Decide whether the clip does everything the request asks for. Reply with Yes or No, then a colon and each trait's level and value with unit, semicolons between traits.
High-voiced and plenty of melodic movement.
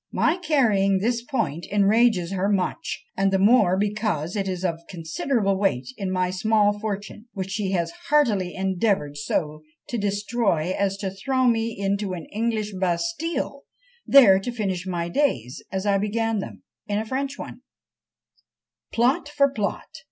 No: high, 200 Hz; average, 3.7 semitones